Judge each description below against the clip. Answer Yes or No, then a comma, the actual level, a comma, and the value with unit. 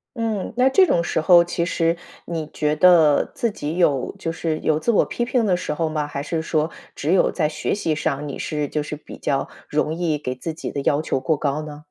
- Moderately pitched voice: Yes, medium, 160 Hz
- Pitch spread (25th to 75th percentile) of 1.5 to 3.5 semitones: Yes, average, 2.7 semitones